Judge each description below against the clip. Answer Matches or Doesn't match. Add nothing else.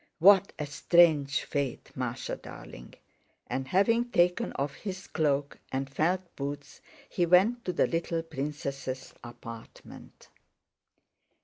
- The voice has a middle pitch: Matches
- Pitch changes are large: Doesn't match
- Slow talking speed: Matches